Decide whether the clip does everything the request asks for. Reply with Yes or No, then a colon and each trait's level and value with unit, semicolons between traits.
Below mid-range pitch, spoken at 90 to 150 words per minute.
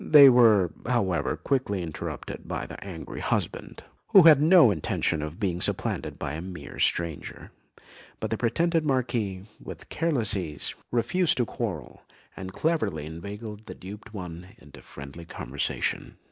Yes: low, 100 Hz; average, 145 wpm